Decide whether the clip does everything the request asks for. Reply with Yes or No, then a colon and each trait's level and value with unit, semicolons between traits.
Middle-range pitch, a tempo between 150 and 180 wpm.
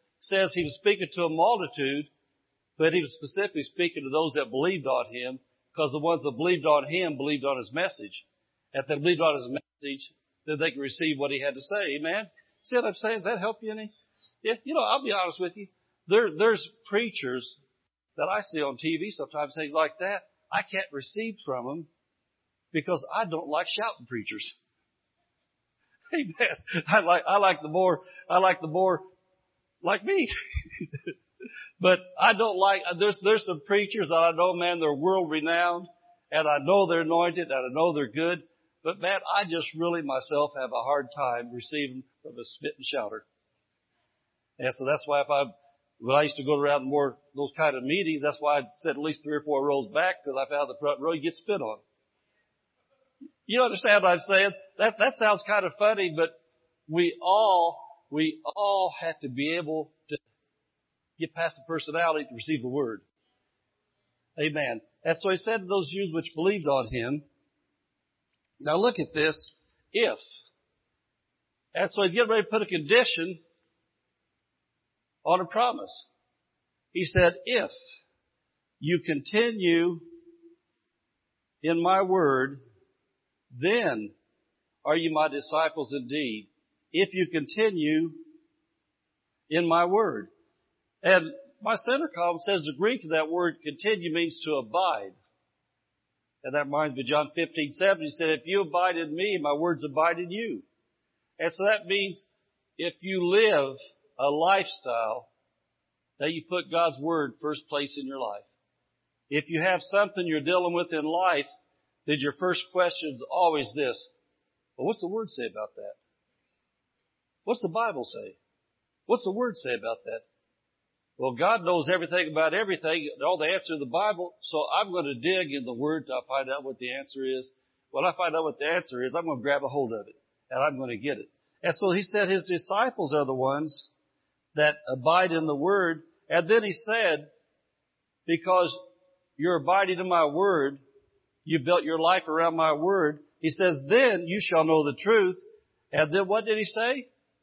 Yes: medium, 170 Hz; average, 175 wpm